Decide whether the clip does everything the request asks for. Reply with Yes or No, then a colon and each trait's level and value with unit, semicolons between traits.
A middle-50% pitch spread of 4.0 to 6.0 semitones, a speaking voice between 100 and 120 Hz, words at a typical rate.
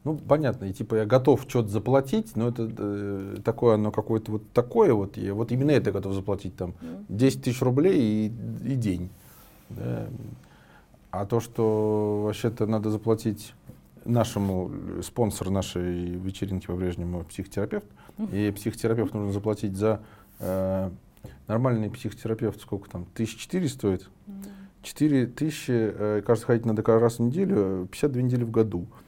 No: average, 3.1 semitones; low, 110 Hz; average, 145 wpm